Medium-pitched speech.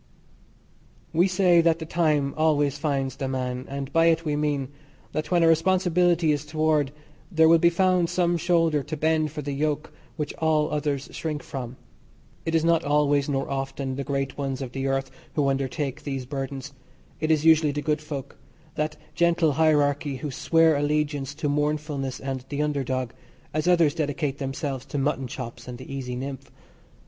Yes: medium, 145 Hz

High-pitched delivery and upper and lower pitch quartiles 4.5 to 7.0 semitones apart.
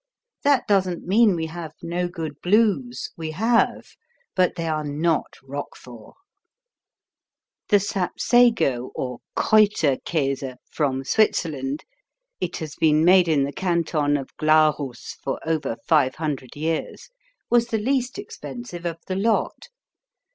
No: medium, 165 Hz; wide, 5.4 semitones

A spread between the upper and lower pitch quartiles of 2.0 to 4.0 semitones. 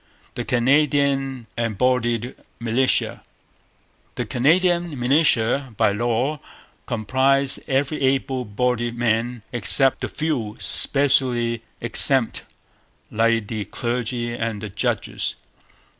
Yes: average, 2.8 semitones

